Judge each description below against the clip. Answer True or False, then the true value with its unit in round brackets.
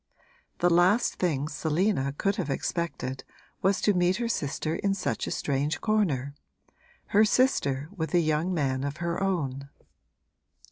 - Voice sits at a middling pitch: True (170 Hz)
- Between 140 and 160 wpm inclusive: True (145 wpm)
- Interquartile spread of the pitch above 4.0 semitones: True (5.4 semitones)